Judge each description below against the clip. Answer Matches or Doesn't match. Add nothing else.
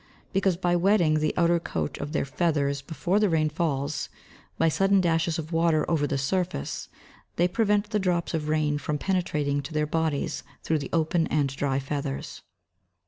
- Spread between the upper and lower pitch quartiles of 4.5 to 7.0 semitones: Doesn't match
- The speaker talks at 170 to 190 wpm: Matches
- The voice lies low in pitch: Doesn't match